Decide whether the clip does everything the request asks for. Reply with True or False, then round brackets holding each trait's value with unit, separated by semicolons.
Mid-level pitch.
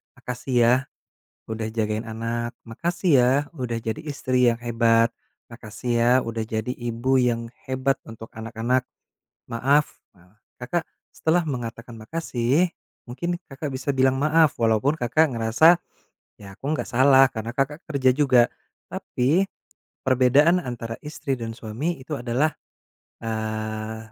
False (125 Hz)